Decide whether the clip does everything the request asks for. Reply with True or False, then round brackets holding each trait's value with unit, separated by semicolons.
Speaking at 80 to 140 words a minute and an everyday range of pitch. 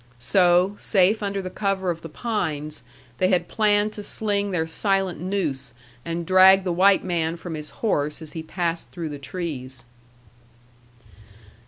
False (155 wpm; 3.5 semitones)